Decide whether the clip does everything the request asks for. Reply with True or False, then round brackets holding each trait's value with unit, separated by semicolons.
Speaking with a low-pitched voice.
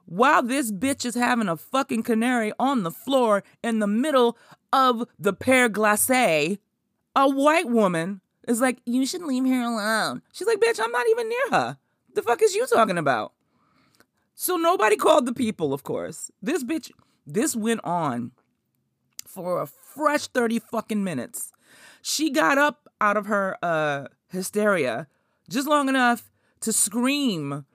False (245 Hz)